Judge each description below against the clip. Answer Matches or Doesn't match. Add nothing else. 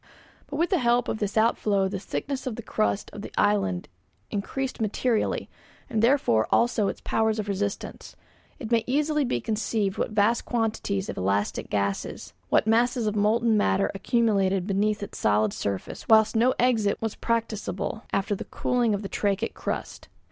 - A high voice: Matches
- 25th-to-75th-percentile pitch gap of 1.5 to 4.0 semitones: Matches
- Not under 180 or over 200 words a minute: Doesn't match